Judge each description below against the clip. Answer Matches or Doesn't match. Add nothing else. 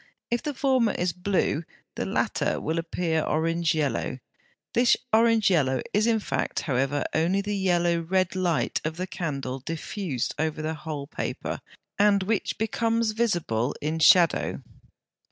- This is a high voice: Doesn't match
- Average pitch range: Matches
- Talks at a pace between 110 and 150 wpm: Matches